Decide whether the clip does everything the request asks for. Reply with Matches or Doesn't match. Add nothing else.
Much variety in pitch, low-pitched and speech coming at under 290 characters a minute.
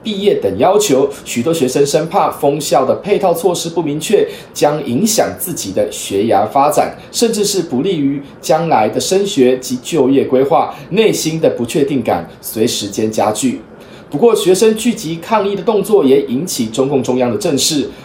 Doesn't match